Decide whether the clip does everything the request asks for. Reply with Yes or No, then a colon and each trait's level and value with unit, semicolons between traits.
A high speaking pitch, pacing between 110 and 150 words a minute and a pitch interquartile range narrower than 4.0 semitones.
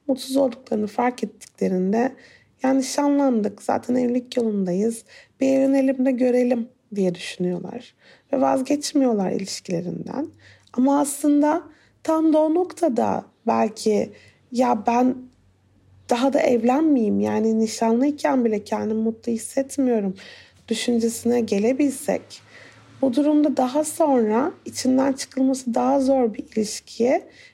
No: very high, 250 Hz; average, 100 wpm; average, 3.5 semitones